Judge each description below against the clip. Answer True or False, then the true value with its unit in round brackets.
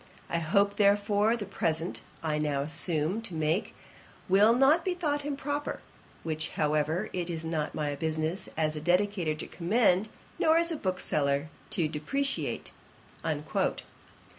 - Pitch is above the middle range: False (175 Hz)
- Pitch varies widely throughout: True (5.8 semitones)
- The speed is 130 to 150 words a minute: True (140 wpm)